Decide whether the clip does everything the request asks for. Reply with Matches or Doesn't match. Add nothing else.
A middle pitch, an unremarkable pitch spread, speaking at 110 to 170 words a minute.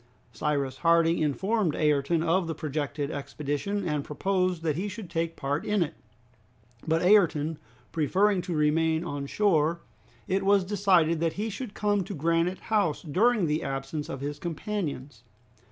Matches